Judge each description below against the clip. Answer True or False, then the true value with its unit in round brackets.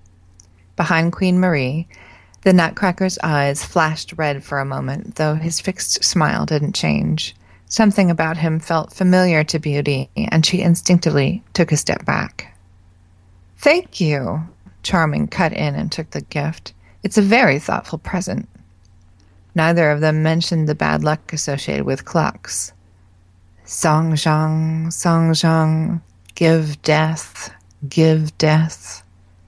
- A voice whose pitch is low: False (155 Hz)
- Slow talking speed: True (130 wpm)